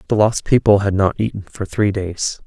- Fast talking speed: Yes, fast, 220 wpm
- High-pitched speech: No, low, 100 Hz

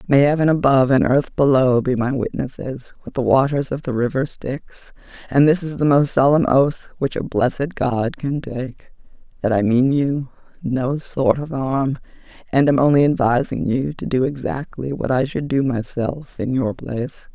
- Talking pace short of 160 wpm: No, average, 175 wpm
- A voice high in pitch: No, low, 135 Hz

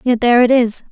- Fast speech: Yes, fast, 265 wpm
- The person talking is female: Yes, female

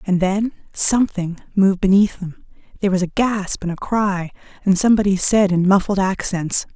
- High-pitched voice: Yes, high, 195 Hz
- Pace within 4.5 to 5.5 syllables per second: Yes, 5.2 syllables/s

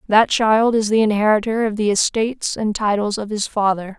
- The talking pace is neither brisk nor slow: Yes, average, 195 wpm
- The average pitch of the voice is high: Yes, high, 215 Hz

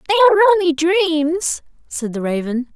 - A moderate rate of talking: Yes, average, 150 wpm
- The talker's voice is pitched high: Yes, very high, 325 Hz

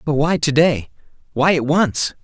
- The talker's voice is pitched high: No, medium, 150 Hz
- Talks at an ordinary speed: Yes, average, 190 wpm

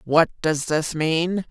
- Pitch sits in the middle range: Yes, medium, 160 Hz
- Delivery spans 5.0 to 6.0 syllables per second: No, 3.2 syllables/s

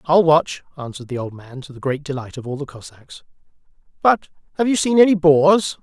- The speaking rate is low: No, fast, 205 wpm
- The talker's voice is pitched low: No, medium, 155 Hz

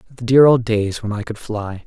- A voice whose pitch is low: Yes, low, 110 Hz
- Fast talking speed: Yes, fast, 260 wpm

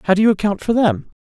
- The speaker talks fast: Yes, fast, 290 wpm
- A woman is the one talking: Yes, female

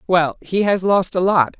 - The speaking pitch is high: No, medium, 180 Hz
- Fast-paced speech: No, average, 190 wpm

